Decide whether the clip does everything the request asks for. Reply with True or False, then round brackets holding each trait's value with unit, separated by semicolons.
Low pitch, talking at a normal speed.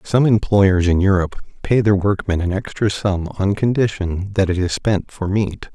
True (100 Hz; 190 wpm)